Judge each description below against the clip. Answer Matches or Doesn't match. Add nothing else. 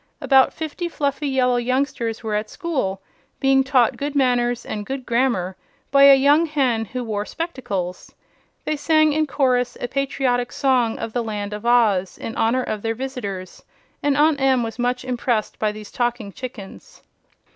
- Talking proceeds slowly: Doesn't match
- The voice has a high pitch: Matches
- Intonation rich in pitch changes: Doesn't match